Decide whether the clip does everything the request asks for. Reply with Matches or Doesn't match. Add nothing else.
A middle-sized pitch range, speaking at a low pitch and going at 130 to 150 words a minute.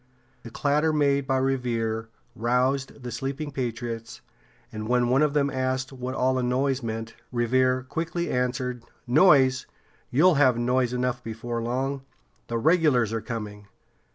Doesn't match